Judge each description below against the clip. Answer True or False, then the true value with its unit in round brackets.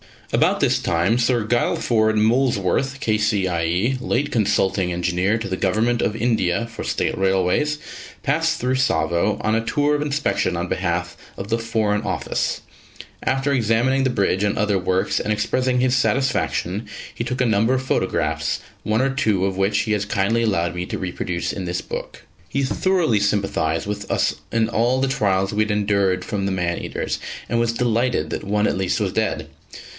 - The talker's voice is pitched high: False (110 Hz)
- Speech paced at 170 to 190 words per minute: True (180 wpm)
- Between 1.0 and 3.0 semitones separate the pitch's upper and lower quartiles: False (4.3 semitones)